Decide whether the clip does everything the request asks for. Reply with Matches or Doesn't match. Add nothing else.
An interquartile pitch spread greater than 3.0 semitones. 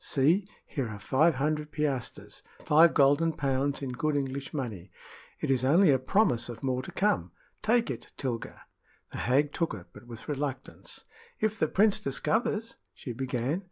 Matches